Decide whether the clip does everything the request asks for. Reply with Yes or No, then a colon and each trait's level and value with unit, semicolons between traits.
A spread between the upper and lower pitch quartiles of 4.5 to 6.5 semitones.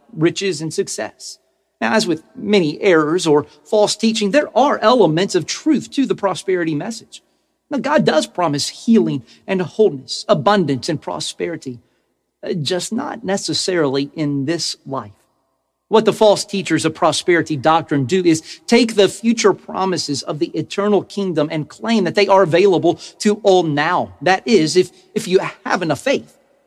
Yes: average, 4.9 semitones